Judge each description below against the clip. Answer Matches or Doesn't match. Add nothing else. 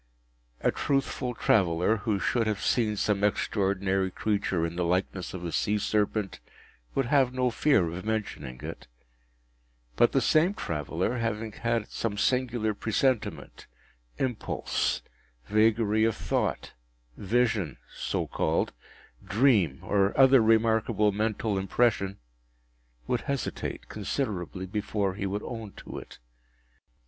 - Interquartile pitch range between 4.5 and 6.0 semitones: Doesn't match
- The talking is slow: Matches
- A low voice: Matches